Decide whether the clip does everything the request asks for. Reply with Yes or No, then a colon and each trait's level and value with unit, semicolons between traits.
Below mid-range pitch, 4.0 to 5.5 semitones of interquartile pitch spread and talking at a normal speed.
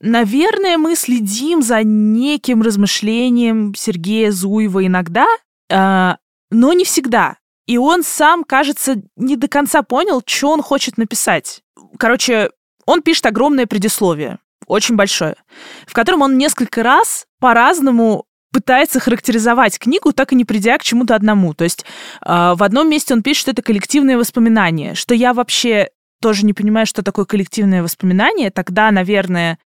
No: high, 235 Hz; average, 4.7 semitones; average, 140 wpm